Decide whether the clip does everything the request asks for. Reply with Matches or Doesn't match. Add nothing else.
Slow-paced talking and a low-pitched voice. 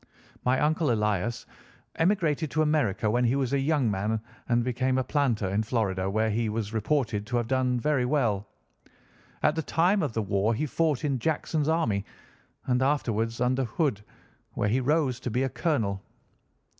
Doesn't match